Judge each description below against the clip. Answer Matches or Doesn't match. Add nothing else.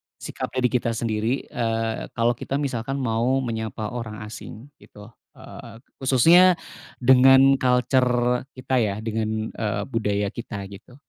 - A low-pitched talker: Matches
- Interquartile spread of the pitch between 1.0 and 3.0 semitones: Matches